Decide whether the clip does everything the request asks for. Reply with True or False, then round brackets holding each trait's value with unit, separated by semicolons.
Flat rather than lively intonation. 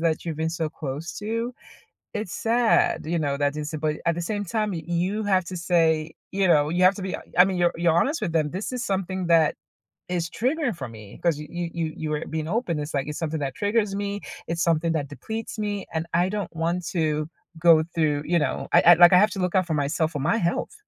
False (3.7 semitones)